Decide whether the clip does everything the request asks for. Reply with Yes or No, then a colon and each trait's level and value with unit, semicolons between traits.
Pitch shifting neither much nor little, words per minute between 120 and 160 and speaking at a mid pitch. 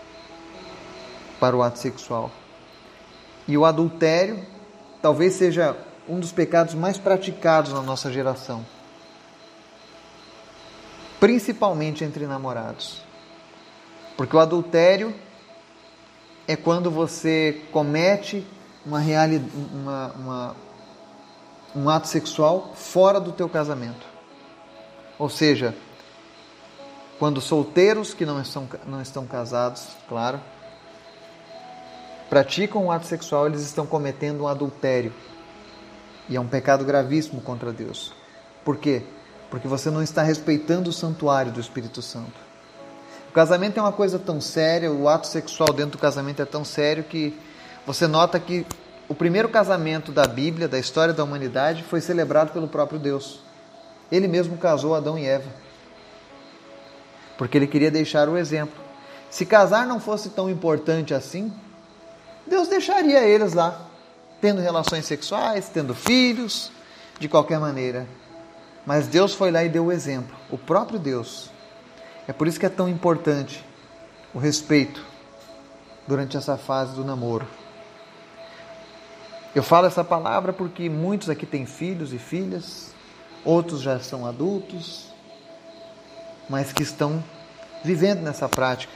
Yes: average, 4.3 semitones; average, 125 wpm; medium, 155 Hz